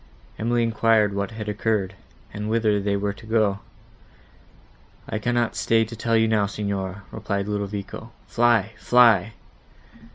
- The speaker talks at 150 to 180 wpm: No, slow, 135 wpm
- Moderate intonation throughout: No, narrow, 2.1 semitones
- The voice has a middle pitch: No, low, 105 Hz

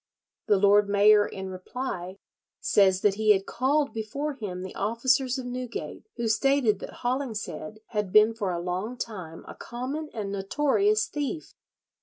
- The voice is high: Yes, high, 220 Hz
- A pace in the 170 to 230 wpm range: No, average, 155 wpm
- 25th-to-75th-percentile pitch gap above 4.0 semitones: Yes, average, 4.8 semitones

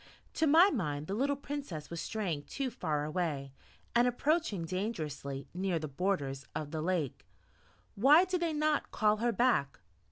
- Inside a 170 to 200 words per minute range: No, average, 160 wpm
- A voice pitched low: No, high, 190 Hz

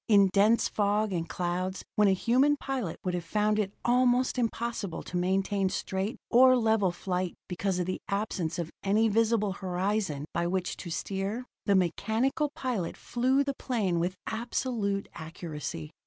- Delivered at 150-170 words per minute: Yes, average, 155 wpm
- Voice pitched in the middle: No, high, 200 Hz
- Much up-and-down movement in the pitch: No, average, 4.1 semitones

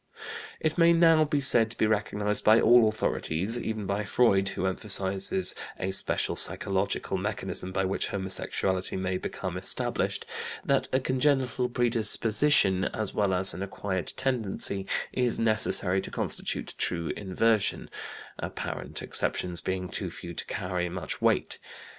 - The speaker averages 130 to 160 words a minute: Yes, average, 140 wpm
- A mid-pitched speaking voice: No, low, 100 Hz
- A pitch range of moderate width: Yes, average, 4.2 semitones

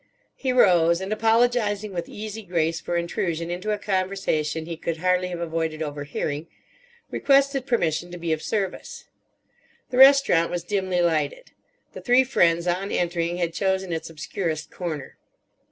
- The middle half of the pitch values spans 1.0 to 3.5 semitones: No, average, 3.9 semitones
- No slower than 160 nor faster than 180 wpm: No, average, 150 wpm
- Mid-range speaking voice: Yes, medium, 175 Hz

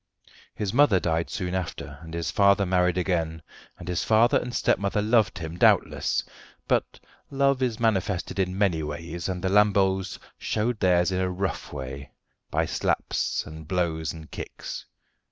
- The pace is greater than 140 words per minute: Yes, average, 155 wpm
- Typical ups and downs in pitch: Yes, average, 3.6 semitones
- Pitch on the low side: Yes, very low, 95 Hz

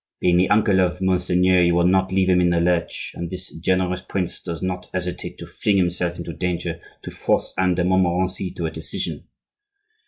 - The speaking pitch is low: Yes, very low, 90 Hz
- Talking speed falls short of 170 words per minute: No, average, 195 wpm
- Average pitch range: No, narrow, 1.1 semitones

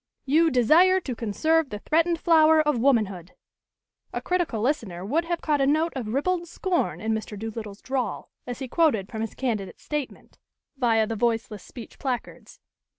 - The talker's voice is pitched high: Yes, very high, 260 Hz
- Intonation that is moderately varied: No, wide, 6.3 semitones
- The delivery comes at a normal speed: Yes, average, 165 wpm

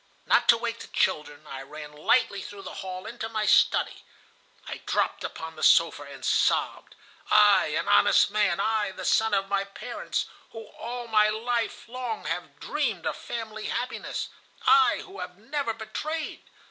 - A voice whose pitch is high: Yes, high, 215 Hz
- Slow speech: No, average, 165 wpm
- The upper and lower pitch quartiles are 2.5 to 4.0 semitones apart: No, average, 4.7 semitones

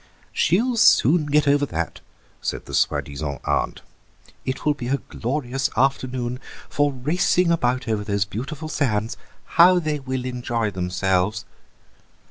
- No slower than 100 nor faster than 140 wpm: Yes, slow, 135 wpm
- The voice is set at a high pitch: No, low, 130 Hz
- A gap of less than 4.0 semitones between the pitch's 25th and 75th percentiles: No, wide, 5.5 semitones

